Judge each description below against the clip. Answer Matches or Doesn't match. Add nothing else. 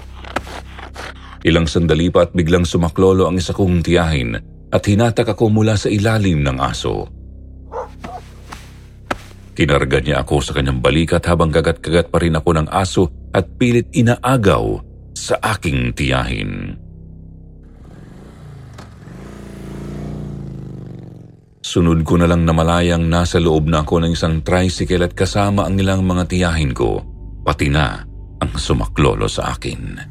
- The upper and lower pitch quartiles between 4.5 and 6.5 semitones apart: Doesn't match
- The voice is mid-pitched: Doesn't match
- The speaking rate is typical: Matches